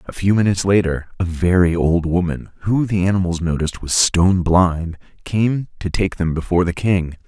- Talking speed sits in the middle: Yes, average, 180 wpm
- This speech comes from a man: Yes, male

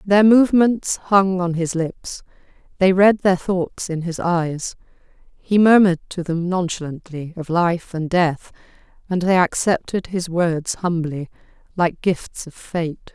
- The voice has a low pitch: No, medium, 180 Hz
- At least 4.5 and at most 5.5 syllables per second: No, 3.9 syllables/s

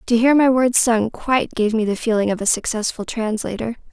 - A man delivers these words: No, female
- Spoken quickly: Yes, fast, 215 wpm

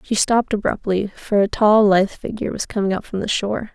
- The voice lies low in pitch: No, high, 205 Hz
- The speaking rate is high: Yes, fast, 225 wpm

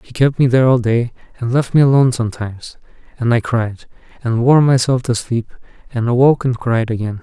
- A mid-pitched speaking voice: No, low, 120 Hz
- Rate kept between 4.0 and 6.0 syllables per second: Yes, 5.9 syllables/s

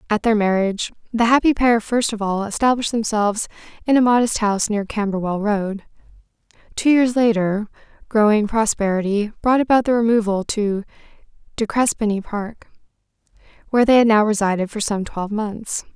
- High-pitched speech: Yes, high, 215 Hz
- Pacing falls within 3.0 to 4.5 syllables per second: No, 5.5 syllables/s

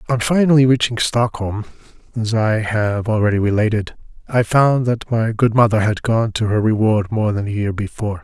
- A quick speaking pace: No, average, 180 wpm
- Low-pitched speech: Yes, low, 110 Hz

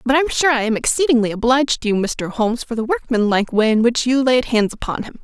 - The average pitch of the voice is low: No, high, 240 Hz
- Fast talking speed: Yes, fast, 250 wpm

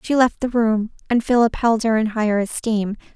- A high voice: Yes, high, 225 Hz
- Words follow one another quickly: Yes, fast, 210 wpm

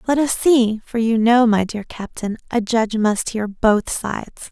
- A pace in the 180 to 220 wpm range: Yes, average, 200 wpm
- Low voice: No, high, 225 Hz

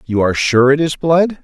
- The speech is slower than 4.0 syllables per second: No, 5.3 syllables/s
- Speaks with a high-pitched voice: No, medium, 145 Hz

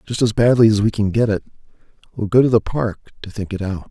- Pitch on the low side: Yes, low, 110 Hz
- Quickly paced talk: Yes, fast, 260 wpm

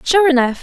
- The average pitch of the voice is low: No, very high, 300 Hz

